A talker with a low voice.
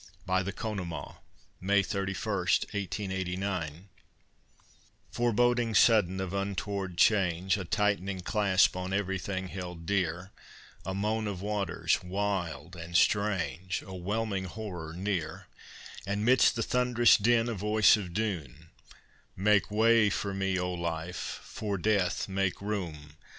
Yes: very low, 95 Hz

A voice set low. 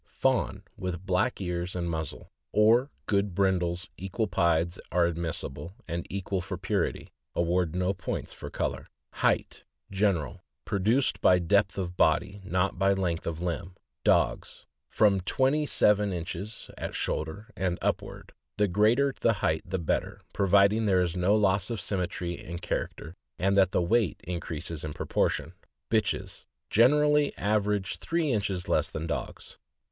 Yes: very low, 95 Hz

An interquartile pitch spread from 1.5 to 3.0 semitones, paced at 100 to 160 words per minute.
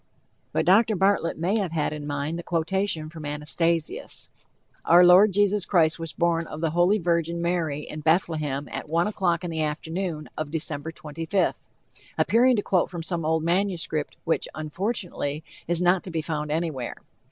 No: narrow, 2.6 semitones; average, 170 wpm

